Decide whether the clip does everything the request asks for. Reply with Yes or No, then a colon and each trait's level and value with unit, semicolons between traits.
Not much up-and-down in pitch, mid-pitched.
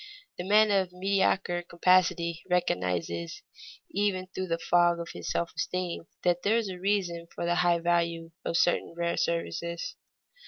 Yes: narrow, 1.6 semitones; medium, 175 Hz